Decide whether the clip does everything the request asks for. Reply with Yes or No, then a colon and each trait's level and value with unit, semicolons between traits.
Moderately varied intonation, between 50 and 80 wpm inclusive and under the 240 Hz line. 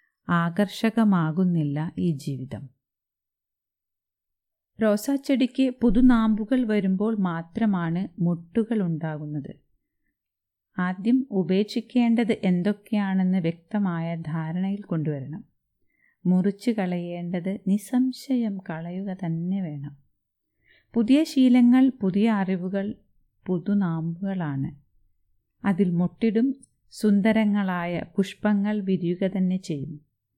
Yes: average, 4.8 semitones; average, 65 wpm; high, 190 Hz